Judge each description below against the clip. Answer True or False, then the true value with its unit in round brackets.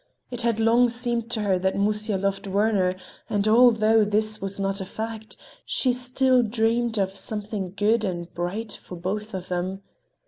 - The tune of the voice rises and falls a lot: False (2.8 semitones)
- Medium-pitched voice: False (215 Hz)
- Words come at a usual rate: True (170 wpm)